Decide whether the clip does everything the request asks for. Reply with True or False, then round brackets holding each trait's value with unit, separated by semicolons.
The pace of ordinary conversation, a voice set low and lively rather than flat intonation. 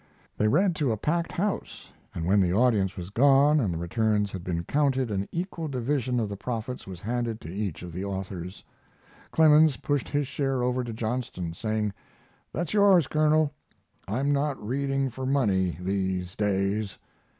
True (170 wpm; 115 Hz; 6.5 semitones)